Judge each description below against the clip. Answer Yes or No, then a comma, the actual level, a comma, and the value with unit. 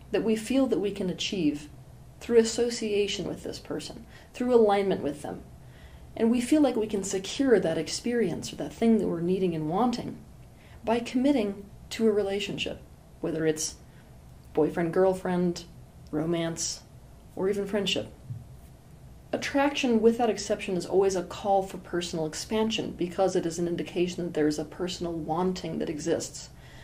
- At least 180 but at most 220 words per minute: No, average, 155 wpm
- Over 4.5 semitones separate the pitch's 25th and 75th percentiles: Yes, average, 5.1 semitones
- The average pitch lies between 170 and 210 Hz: Yes, high, 190 Hz